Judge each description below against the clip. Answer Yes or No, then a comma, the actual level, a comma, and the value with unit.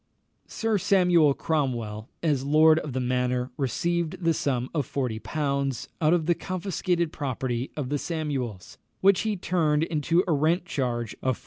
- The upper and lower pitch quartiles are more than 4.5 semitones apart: Yes, average, 4.9 semitones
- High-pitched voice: No, medium, 150 Hz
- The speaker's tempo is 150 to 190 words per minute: Yes, average, 155 wpm